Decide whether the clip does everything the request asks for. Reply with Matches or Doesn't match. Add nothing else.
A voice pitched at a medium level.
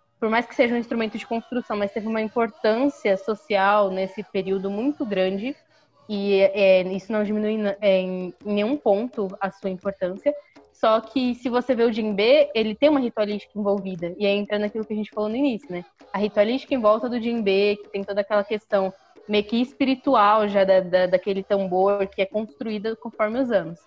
Doesn't match